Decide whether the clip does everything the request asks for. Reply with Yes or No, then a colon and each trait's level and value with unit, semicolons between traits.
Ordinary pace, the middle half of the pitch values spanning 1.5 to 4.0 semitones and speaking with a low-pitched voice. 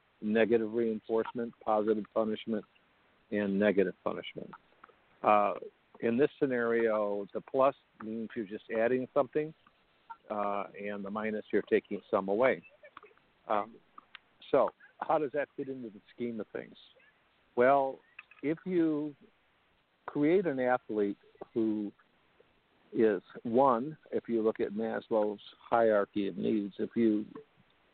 No: slow, 120 wpm; average, 3.1 semitones; low, 110 Hz